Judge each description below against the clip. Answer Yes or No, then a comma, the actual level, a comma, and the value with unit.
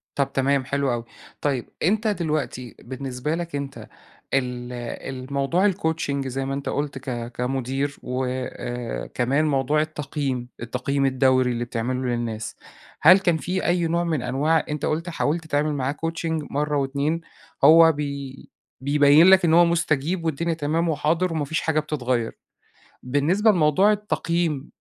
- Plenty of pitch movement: No, average, 3.8 semitones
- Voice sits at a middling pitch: Yes, medium, 145 Hz